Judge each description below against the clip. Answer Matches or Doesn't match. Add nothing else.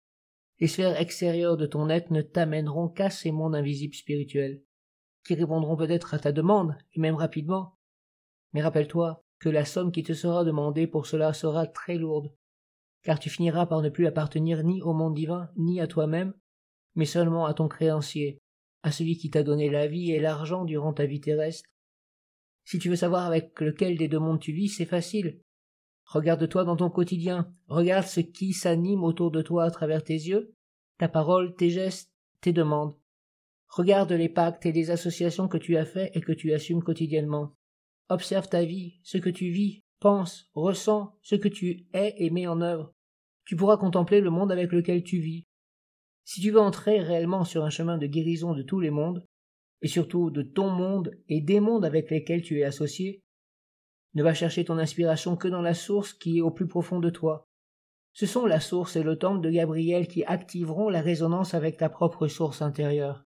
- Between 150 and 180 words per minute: Doesn't match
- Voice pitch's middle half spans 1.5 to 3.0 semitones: Matches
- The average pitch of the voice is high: Doesn't match